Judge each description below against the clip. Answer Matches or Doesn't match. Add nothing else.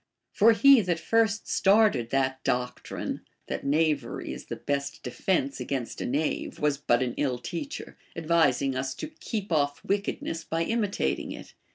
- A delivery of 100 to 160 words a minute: Matches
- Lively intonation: Matches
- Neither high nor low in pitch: Matches